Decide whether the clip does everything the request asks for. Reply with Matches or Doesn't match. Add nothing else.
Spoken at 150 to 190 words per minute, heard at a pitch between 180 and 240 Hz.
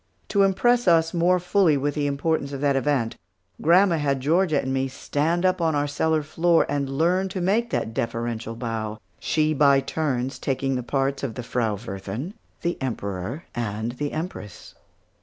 Doesn't match